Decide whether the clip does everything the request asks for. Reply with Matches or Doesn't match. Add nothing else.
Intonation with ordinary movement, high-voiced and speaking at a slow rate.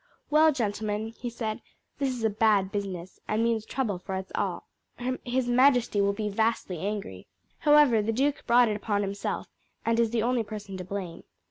Doesn't match